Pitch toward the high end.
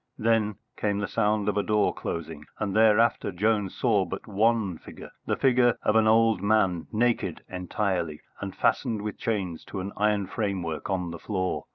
No: low, 105 Hz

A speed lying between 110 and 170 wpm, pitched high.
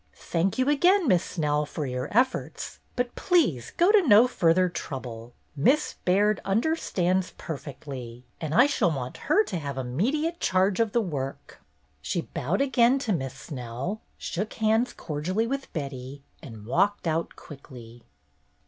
No: average, 150 wpm; medium, 180 Hz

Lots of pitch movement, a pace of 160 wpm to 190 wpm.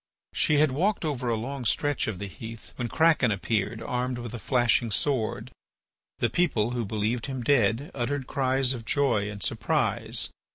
No: average, 3.7 semitones; average, 170 wpm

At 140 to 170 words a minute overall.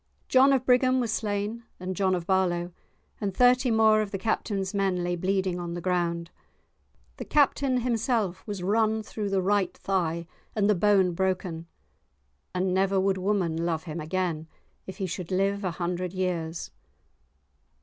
Yes: average, 160 wpm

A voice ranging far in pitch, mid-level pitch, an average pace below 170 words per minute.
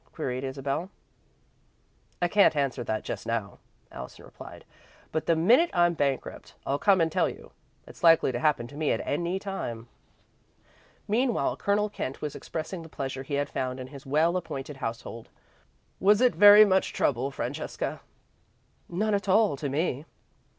Yes: wide, 6.1 semitones; medium, 155 Hz; average, 155 wpm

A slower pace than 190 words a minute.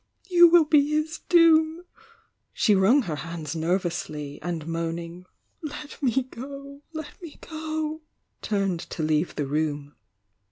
Yes: average, 155 wpm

